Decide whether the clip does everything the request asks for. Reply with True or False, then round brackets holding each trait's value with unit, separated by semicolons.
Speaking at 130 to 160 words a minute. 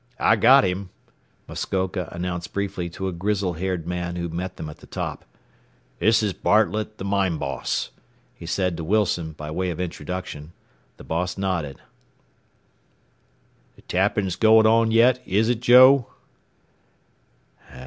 True (140 wpm)